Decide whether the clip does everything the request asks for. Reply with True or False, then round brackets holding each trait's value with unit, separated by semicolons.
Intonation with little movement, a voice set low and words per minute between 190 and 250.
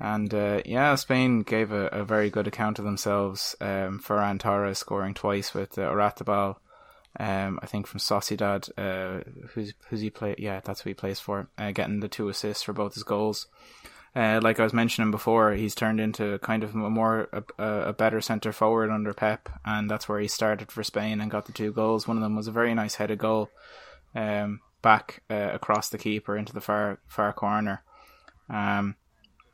True (1.3 semitones; 105 Hz; 200 wpm)